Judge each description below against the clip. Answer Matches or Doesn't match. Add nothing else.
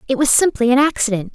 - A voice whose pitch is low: Doesn't match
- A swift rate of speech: Matches